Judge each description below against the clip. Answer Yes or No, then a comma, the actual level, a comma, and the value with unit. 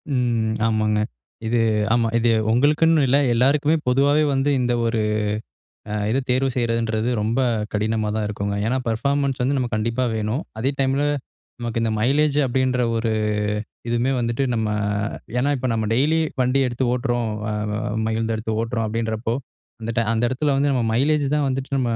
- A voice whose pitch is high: No, low, 120 Hz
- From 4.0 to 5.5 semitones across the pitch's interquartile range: No, average, 3.2 semitones